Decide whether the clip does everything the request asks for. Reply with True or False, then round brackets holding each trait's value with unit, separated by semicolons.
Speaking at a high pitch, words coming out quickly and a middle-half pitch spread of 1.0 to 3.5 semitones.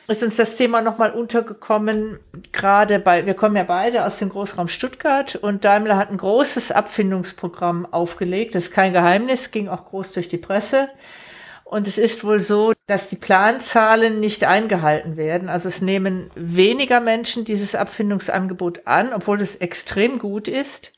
False (205 Hz; 165 wpm; 3.1 semitones)